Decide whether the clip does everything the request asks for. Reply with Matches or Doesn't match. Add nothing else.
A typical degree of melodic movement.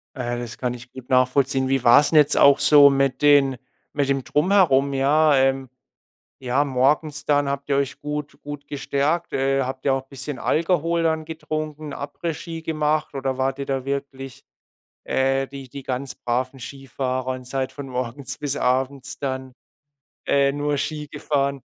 Doesn't match